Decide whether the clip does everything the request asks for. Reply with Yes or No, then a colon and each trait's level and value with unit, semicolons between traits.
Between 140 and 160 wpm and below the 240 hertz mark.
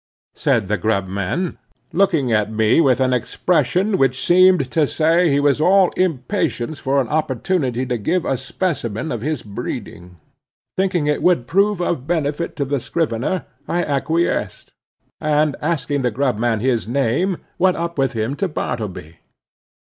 Yes: average, 155 wpm; medium, 140 Hz